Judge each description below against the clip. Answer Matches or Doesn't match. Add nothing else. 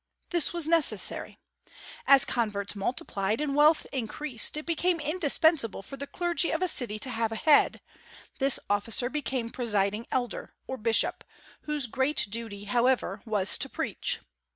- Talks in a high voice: Matches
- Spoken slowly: Doesn't match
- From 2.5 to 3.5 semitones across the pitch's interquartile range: Doesn't match